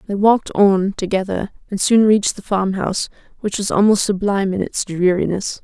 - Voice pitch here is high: Yes, high, 200 Hz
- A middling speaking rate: Yes, average, 170 wpm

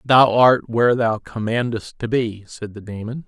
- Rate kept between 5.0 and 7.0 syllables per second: No, 4.5 syllables/s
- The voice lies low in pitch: Yes, low, 115 Hz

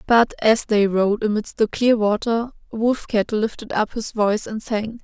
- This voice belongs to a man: No, female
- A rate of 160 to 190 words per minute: Yes, average, 180 wpm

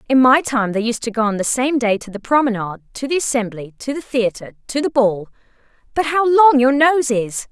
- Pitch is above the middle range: Yes, high, 245 Hz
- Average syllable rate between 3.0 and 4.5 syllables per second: No, 5.4 syllables/s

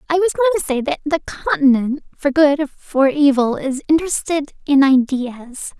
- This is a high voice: Yes, very high, 290 Hz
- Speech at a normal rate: Yes, average, 175 wpm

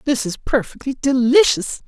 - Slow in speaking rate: Yes, slow, 130 wpm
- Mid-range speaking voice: No, very high, 260 Hz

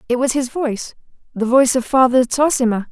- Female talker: Yes, female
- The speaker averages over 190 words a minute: No, average, 185 wpm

